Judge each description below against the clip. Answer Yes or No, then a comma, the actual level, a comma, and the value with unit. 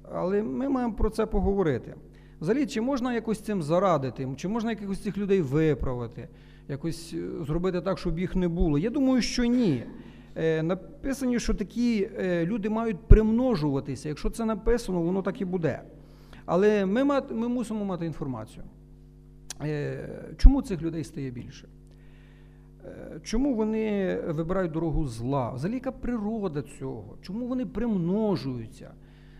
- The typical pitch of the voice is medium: No, high, 195 Hz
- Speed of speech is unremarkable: Yes, average, 135 wpm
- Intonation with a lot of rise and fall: Yes, wide, 6.0 semitones